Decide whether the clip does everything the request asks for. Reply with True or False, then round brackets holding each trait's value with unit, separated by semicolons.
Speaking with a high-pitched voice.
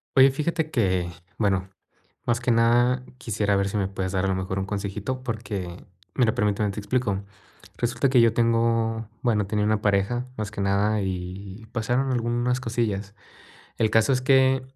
False (110 Hz)